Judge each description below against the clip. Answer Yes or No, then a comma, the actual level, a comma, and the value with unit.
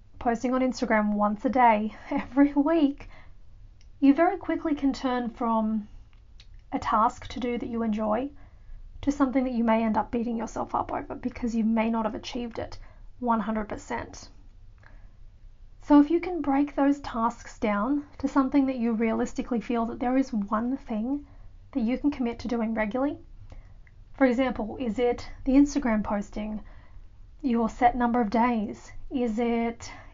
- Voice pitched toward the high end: Yes, high, 235 Hz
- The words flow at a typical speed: Yes, average, 160 wpm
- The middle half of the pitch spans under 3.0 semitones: No, average, 3.7 semitones